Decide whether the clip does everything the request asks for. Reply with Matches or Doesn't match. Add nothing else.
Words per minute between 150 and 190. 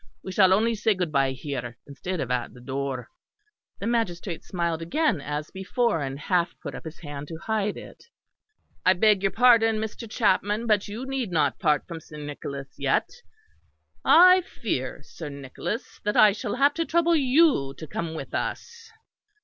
Matches